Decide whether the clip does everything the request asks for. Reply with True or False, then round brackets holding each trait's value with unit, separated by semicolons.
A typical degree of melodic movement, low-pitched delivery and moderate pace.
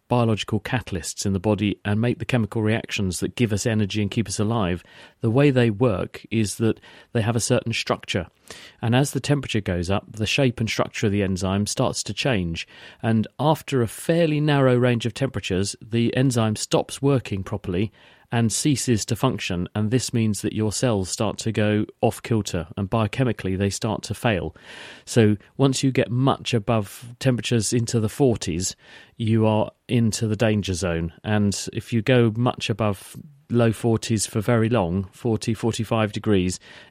True (3.0 semitones; 115 Hz; 175 wpm)